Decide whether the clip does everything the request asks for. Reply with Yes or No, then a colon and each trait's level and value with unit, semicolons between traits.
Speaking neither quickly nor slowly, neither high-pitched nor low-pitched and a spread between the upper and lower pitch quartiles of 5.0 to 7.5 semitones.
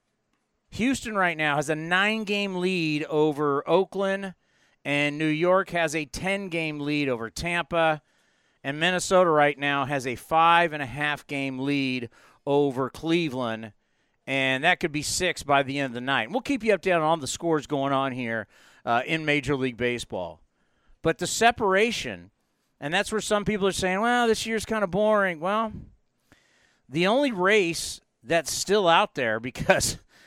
Yes: average, 170 wpm; medium, 160 Hz; wide, 5.4 semitones